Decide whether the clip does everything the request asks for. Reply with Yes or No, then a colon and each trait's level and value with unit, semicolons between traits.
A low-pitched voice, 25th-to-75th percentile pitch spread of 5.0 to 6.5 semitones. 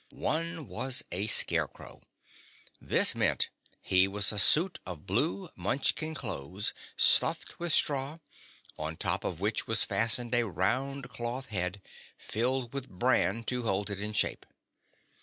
Yes: low, 115 Hz; wide, 5.4 semitones